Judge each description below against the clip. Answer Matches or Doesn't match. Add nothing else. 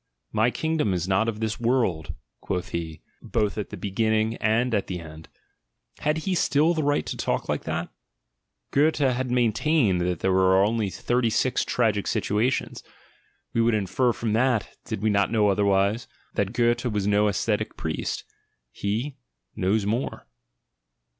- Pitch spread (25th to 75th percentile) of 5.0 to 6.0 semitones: Doesn't match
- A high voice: Doesn't match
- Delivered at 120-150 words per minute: Doesn't match